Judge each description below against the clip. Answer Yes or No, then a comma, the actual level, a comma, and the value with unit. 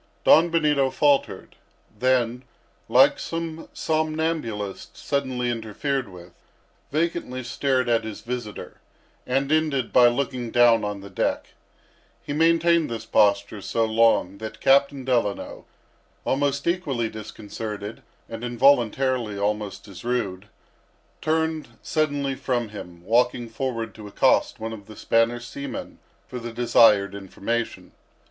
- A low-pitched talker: Yes, low, 120 Hz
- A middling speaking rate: No, slow, 120 wpm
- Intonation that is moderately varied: Yes, average, 4.3 semitones